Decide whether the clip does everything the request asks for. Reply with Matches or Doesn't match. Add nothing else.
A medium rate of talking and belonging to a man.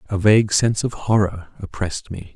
Matches